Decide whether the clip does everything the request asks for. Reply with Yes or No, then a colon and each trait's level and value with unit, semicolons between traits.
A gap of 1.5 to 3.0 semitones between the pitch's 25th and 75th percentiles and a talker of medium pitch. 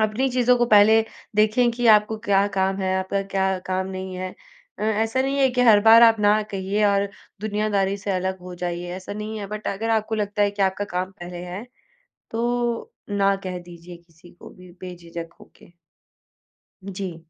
No: average, 2.7 semitones; high, 200 Hz